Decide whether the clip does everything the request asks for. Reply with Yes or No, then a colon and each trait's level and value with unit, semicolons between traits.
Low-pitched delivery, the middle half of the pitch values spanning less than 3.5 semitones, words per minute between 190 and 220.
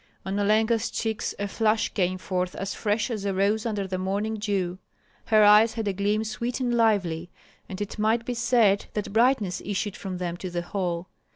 No: high, 205 Hz; average, 2.8 semitones; average, 195 wpm